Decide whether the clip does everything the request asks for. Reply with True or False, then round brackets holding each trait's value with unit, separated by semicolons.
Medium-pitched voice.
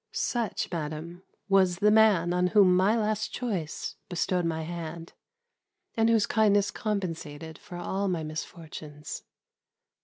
True (180 Hz)